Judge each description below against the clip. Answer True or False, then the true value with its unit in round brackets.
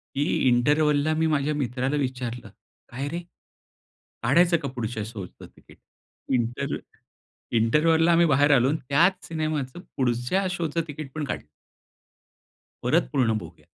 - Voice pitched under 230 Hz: True (140 Hz)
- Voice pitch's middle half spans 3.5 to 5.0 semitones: True (4.2 semitones)